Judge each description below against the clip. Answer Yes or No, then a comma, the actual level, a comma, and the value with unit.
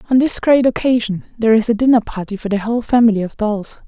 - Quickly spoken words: Yes, fast, 230 wpm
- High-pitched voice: Yes, high, 225 Hz